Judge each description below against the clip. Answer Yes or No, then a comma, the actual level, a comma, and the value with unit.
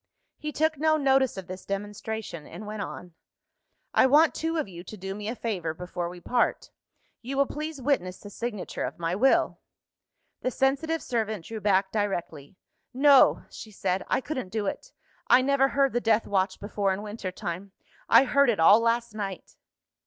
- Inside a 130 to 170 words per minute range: No, average, 180 wpm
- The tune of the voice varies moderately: No, wide, 5.8 semitones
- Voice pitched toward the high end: Yes, high, 215 Hz